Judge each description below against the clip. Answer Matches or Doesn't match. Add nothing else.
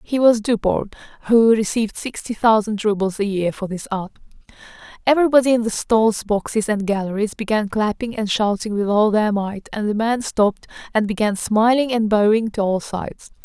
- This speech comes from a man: Doesn't match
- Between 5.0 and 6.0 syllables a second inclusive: Doesn't match